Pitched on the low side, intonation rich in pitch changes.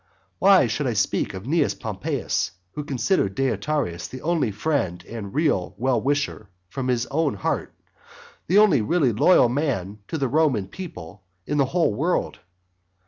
Yes: low, 130 Hz; wide, 6.7 semitones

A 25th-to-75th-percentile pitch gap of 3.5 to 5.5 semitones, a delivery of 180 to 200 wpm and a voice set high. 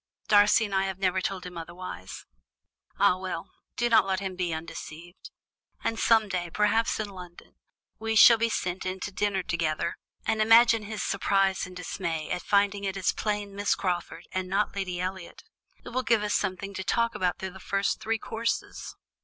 No: narrow, 2.5 semitones; average, 185 wpm; high, 195 Hz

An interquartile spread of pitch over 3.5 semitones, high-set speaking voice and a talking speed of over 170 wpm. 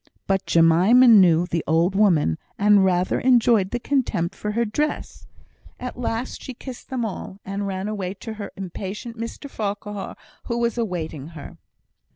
No: average, 4.3 semitones; high, 205 Hz; average, 160 wpm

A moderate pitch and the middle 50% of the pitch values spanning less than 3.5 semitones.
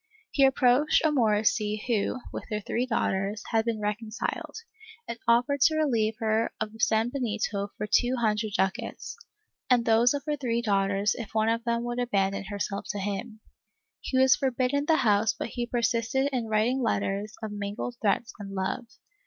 No: high, 225 Hz; average, 2.9 semitones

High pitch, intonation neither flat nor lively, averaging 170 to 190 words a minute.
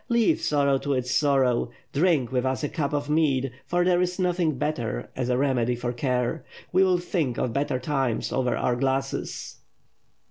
No: low, 135 Hz; average, 3.8 semitones; average, 180 wpm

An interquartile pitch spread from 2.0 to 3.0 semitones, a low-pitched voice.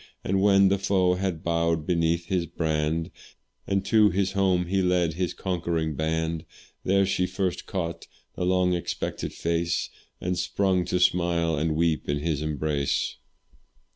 Yes: narrow, 2.4 semitones; very low, 85 Hz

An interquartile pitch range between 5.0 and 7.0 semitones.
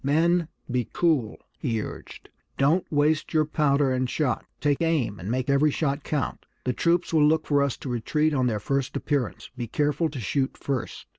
No: average, 3.3 semitones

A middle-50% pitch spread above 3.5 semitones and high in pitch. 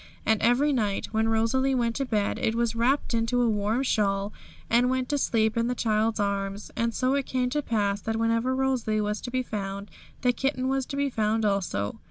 No: average, 3.2 semitones; high, 230 Hz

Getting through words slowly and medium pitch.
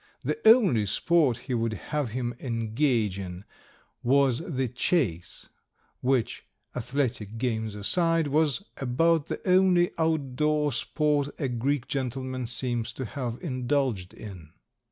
No: slow, 120 wpm; low, 130 Hz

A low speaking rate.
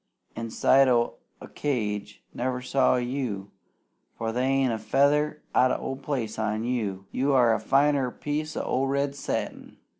No: average, 150 wpm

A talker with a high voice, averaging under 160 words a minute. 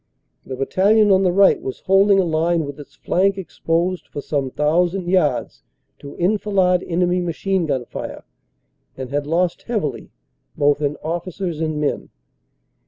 No: medium, 175 Hz; average, 150 wpm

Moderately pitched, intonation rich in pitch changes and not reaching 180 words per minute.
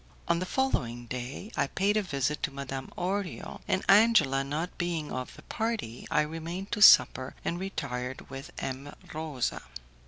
Yes: medium, 150 Hz; wide, 6.0 semitones; average, 160 wpm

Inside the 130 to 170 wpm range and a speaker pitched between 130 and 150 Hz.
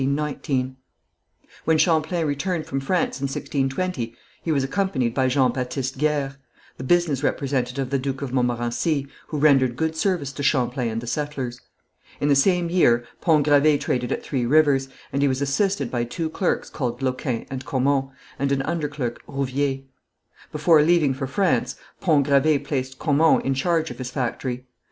Yes: average, 165 wpm; medium, 140 Hz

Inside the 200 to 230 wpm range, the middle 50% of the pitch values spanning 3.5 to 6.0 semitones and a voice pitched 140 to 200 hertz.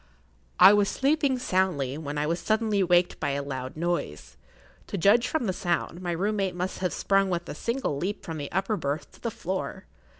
Yes: fast, 205 wpm; average, 4.3 semitones; medium, 185 Hz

